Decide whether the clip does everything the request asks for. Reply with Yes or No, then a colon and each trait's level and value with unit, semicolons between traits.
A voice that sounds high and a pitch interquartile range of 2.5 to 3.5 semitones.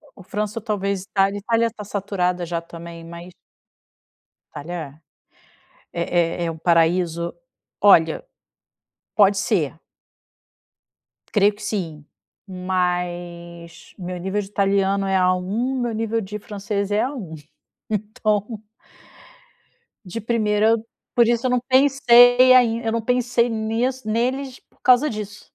No: high, 205 Hz; average, 4.1 semitones